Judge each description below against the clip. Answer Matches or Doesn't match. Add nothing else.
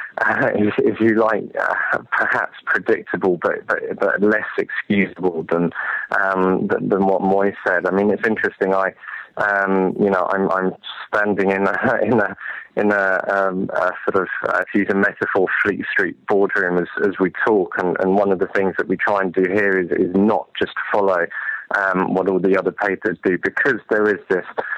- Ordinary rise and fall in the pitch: Doesn't match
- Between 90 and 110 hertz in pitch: Matches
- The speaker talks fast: Doesn't match